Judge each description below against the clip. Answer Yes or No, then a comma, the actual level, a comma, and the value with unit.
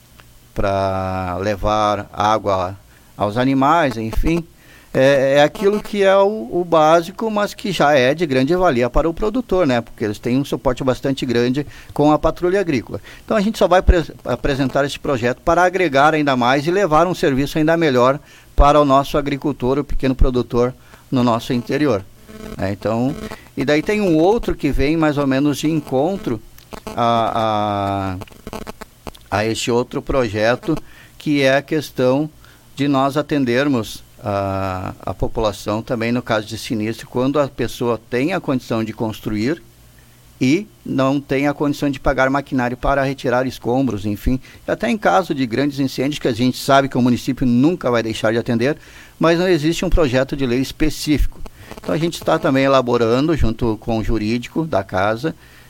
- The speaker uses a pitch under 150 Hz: Yes, low, 135 Hz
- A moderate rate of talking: Yes, average, 170 wpm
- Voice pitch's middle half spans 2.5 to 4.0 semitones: No, average, 4.4 semitones